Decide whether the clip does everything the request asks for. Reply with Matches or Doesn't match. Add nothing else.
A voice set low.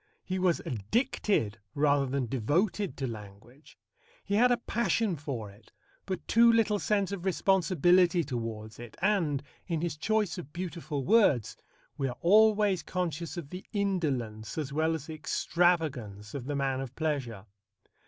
Doesn't match